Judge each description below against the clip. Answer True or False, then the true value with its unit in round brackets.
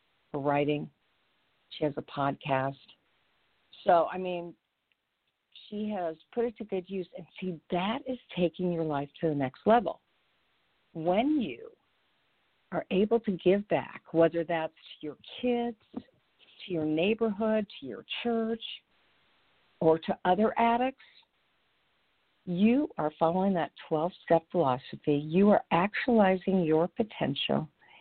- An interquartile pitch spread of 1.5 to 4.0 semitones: False (5.5 semitones)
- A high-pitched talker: False (180 Hz)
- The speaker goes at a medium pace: False (130 wpm)